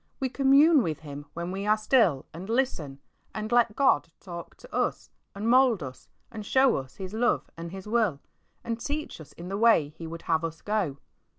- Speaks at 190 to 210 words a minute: Yes, average, 200 wpm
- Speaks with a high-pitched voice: Yes, high, 200 Hz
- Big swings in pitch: Yes, wide, 6.4 semitones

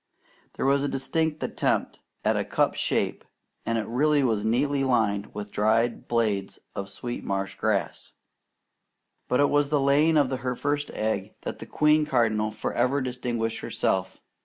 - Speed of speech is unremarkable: Yes, average, 160 wpm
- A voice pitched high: No, low, 125 Hz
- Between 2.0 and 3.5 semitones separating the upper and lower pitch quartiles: No, average, 4.6 semitones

